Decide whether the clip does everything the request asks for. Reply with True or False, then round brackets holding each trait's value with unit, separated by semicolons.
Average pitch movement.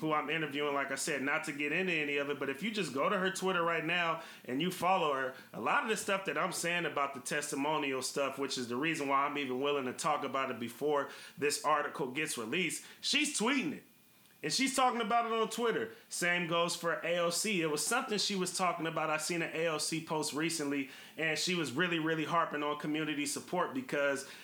True (4.2 semitones)